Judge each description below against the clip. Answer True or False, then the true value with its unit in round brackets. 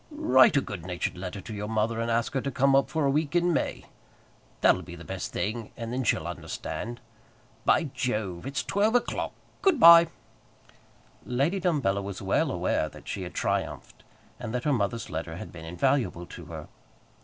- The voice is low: True (120 Hz)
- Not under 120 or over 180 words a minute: False (190 wpm)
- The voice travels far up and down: True (6.1 semitones)